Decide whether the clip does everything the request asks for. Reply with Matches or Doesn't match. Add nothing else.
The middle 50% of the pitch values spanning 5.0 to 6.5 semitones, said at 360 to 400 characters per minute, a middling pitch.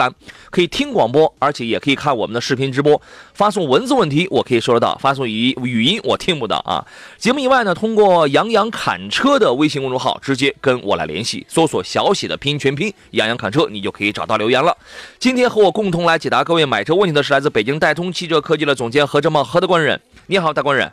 Matches